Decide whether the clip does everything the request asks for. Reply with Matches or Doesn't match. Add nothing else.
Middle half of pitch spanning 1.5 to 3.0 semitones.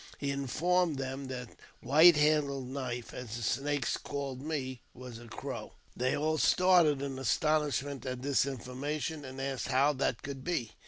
Matches